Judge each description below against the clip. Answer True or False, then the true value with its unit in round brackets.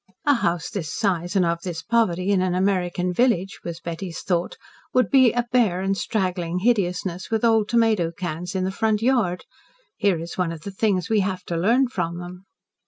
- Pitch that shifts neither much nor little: True (3.9 semitones)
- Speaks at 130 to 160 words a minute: False (195 wpm)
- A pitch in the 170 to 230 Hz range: True (185 Hz)